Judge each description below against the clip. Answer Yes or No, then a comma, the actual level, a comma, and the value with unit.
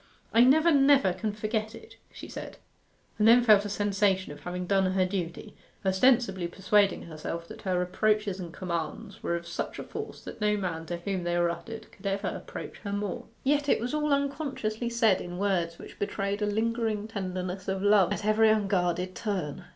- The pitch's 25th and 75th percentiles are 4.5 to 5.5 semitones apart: No, average, 3.4 semitones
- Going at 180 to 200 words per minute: Yes, average, 190 wpm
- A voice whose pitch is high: Yes, high, 200 Hz